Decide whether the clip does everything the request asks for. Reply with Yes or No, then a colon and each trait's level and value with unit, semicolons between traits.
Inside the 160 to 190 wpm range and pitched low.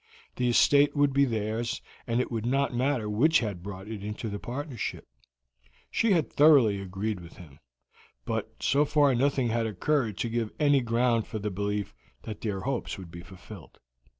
Yes: average, 180 wpm; low, 115 Hz